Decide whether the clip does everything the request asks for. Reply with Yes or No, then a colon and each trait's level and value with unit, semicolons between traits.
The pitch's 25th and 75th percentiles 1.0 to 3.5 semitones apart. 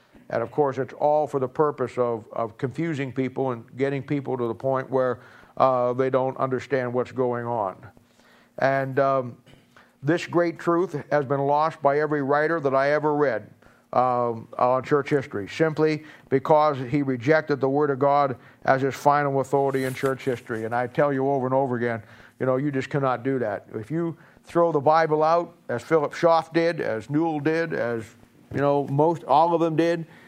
Yes: average, 2.9 semitones